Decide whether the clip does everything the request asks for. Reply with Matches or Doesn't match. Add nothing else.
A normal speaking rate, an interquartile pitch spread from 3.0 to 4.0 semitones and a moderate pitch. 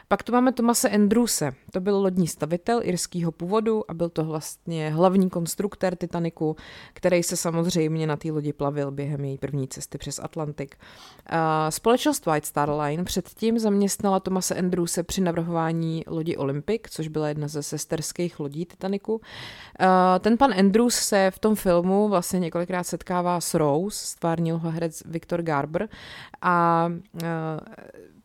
Matches